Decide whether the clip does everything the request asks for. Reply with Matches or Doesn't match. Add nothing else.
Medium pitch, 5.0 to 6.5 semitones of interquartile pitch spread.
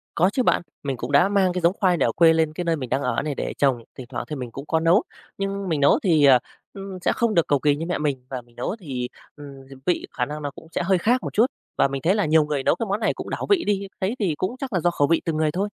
Matches